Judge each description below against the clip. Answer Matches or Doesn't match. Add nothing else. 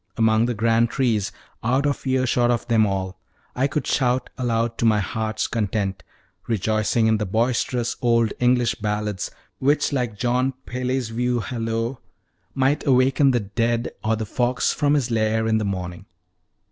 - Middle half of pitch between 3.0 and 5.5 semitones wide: Doesn't match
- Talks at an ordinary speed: Matches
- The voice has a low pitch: Matches